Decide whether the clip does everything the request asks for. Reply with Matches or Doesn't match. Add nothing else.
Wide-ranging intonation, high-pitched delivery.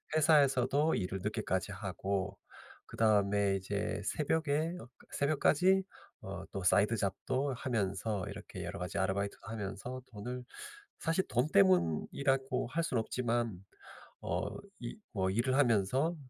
Doesn't match